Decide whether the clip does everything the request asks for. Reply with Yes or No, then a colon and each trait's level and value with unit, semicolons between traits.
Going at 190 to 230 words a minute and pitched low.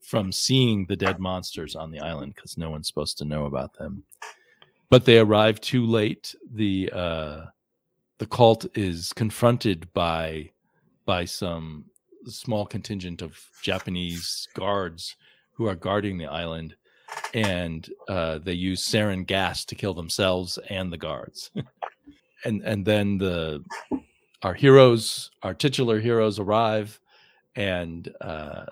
No: slow, 135 wpm; very low, 95 Hz